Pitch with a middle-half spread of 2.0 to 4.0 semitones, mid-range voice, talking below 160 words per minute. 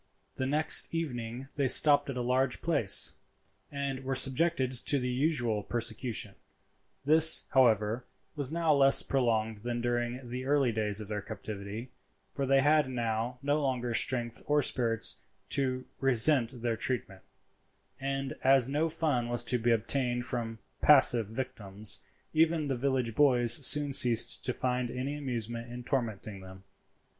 No: average, 2.9 semitones; low, 125 Hz; average, 150 wpm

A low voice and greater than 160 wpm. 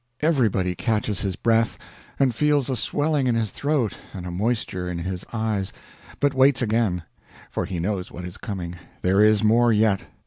Yes: low, 110 Hz; average, 175 wpm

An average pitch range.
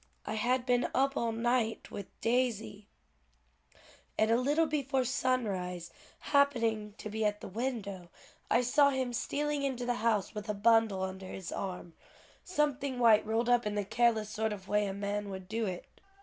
Yes: average, 3.6 semitones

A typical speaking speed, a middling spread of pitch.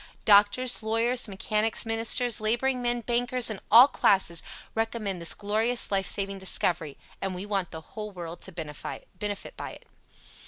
Yes: average, 150 wpm; average, 3.5 semitones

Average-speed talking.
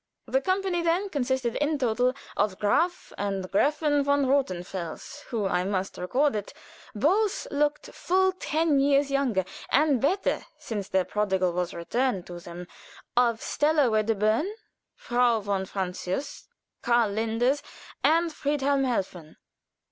No: slow, 130 wpm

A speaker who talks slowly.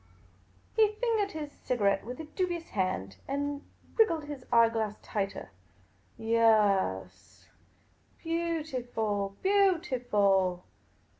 Yes: slow, 100 wpm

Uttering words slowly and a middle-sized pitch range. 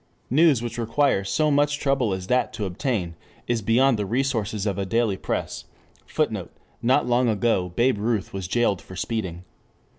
No: average, 170 wpm; average, 4.7 semitones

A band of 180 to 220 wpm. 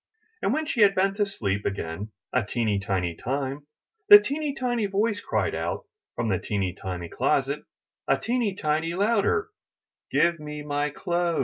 No: average, 165 wpm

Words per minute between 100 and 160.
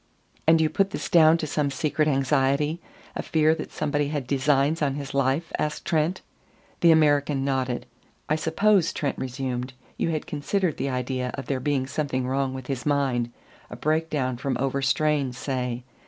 No: average, 170 wpm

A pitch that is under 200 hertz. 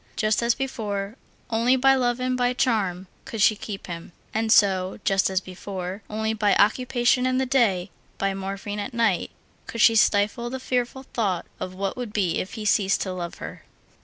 No: high, 215 Hz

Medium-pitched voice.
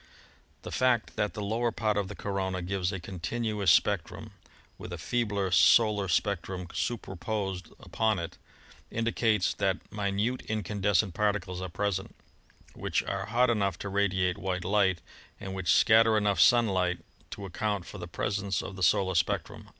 No: low, 100 Hz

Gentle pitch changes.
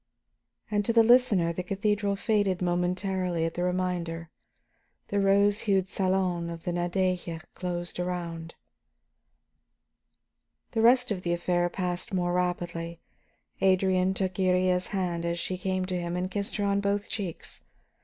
Yes: narrow, 2.1 semitones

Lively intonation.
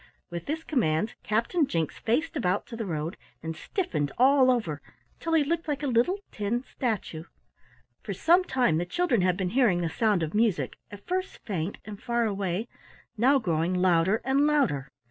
Yes: wide, 7.5 semitones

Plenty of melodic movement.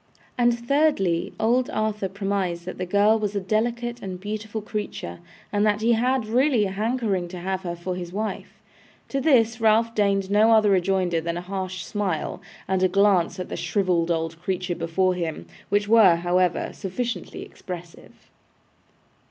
No: average, 3.5 semitones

